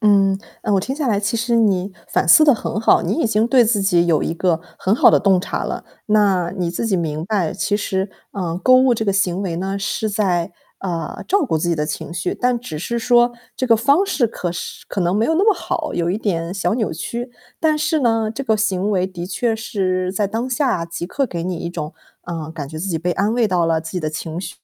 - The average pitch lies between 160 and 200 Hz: Yes, high, 195 Hz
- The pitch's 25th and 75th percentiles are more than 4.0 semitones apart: Yes, average, 4.8 semitones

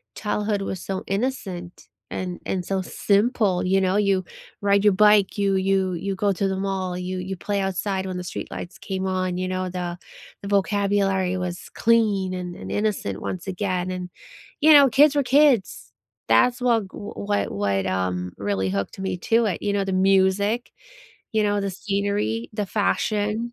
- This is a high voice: Yes, high, 195 Hz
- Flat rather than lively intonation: Yes, narrow, 2.1 semitones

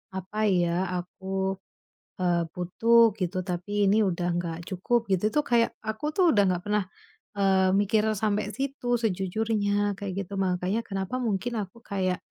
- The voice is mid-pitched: No, high, 200 Hz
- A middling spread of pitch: Yes, average, 3.0 semitones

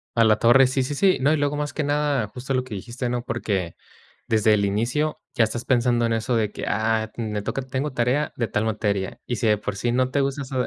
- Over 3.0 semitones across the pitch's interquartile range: Yes, average, 3.6 semitones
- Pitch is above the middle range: No, low, 120 Hz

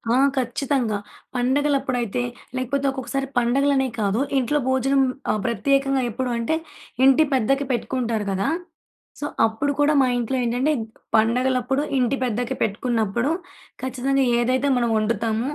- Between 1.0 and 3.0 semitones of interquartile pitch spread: Yes, average, 2.7 semitones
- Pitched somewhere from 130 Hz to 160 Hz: No, very high, 255 Hz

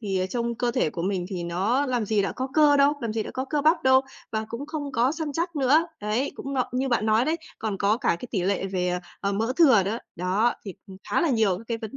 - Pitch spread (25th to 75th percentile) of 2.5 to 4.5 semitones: No, average, 5.3 semitones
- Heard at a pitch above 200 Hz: Yes, high, 230 Hz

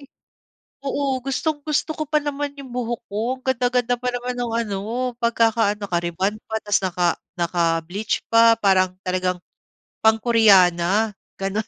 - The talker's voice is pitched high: Yes, high, 225 Hz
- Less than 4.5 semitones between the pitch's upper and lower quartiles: No, average, 4.9 semitones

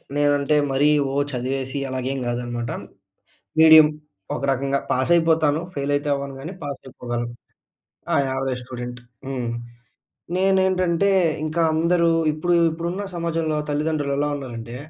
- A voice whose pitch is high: No, medium, 145 Hz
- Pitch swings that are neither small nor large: Yes, average, 3.6 semitones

